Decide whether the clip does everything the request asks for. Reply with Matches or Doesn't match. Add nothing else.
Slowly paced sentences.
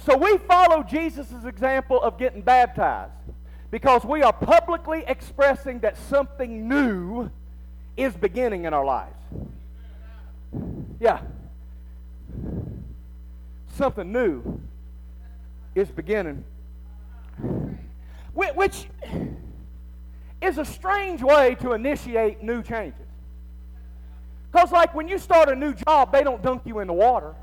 Matches